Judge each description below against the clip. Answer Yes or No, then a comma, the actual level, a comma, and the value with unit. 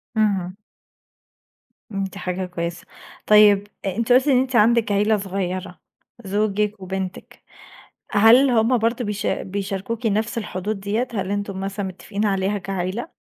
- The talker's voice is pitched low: No, high, 205 Hz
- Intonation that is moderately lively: No, narrow, 2.3 semitones